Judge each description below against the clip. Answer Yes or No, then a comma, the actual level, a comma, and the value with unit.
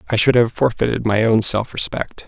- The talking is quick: Yes, fast, 210 wpm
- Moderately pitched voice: No, low, 115 Hz